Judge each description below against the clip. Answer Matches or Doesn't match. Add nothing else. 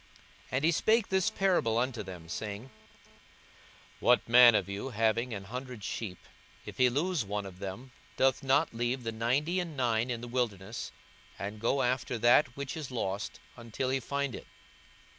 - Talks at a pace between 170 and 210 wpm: Matches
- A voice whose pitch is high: Doesn't match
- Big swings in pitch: Doesn't match